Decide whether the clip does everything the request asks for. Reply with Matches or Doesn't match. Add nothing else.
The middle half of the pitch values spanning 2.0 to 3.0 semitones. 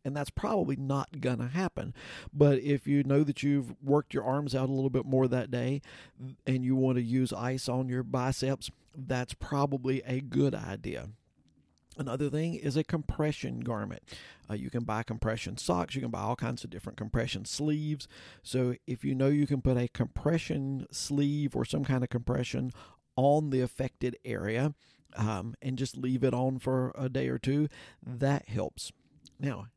Matches